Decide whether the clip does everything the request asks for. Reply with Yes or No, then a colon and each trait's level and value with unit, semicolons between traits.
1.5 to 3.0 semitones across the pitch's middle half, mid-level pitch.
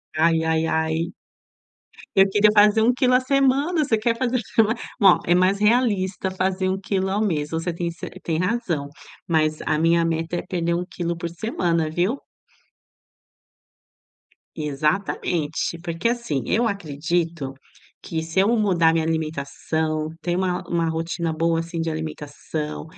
No: average, 3.6 semitones; medium, 170 Hz